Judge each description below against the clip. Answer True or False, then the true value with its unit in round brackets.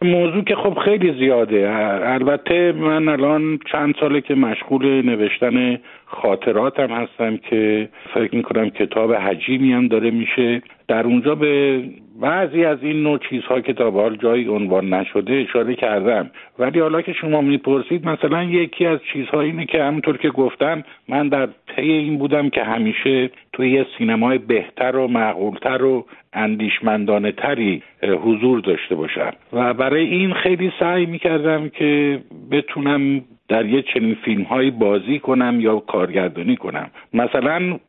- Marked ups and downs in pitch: False (4.6 semitones)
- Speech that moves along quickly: False (140 wpm)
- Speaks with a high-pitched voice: False (135 Hz)